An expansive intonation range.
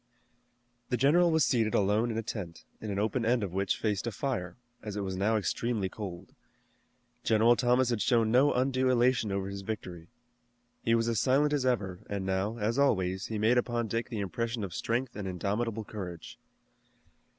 No: average, 3.6 semitones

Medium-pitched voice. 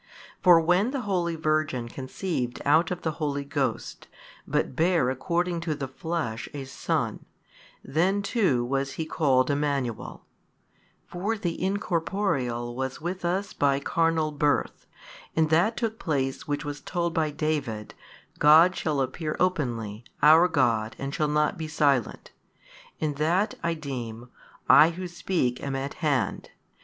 Yes: medium, 155 Hz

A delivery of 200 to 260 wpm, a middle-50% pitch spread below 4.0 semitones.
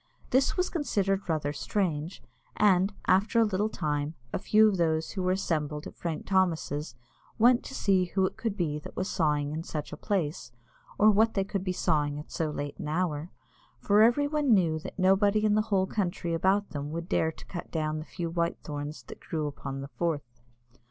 No: fast, 205 wpm; average, 4.8 semitones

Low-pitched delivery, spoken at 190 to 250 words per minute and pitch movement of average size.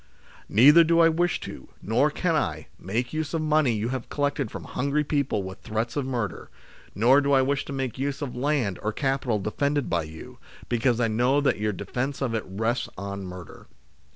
Yes: low, 125 Hz; average, 200 wpm; average, 4.8 semitones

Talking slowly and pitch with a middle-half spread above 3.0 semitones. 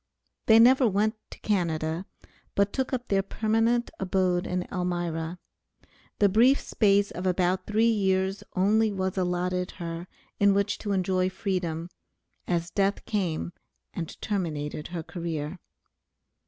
No: slow, 130 wpm; average, 2.7 semitones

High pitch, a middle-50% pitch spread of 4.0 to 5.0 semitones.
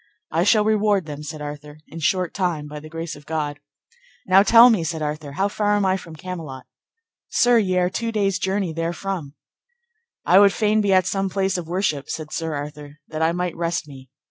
No: medium, 170 Hz; average, 4.3 semitones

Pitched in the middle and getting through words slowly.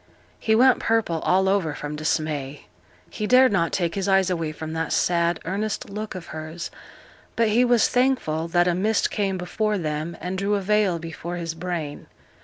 No: medium, 180 Hz; average, 185 wpm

